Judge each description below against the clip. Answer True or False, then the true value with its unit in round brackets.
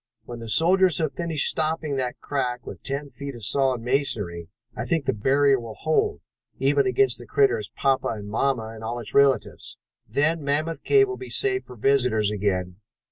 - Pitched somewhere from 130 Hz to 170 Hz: True (135 Hz)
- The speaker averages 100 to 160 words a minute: False (185 wpm)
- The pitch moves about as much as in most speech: True (4.2 semitones)